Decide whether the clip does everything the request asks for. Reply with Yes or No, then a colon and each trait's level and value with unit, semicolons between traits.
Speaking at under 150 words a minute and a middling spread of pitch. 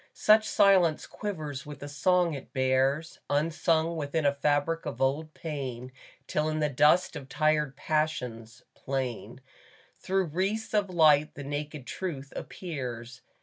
Yes: average, 140 wpm; average, 3.3 semitones